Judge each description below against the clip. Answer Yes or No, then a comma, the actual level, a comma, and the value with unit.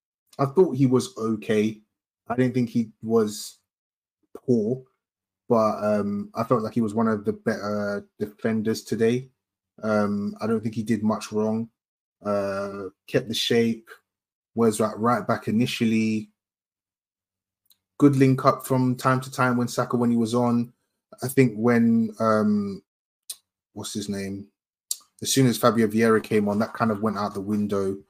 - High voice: No, low, 110 Hz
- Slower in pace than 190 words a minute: Yes, average, 160 wpm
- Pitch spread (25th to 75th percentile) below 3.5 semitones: Yes, average, 2.7 semitones